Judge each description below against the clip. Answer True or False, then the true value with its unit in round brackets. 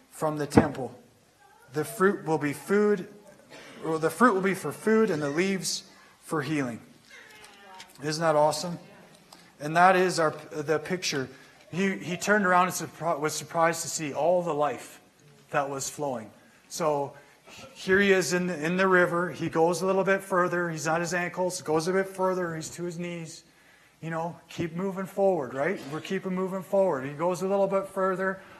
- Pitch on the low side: False (175 Hz)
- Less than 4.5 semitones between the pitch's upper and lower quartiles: True (3.4 semitones)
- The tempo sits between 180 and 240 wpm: True (185 wpm)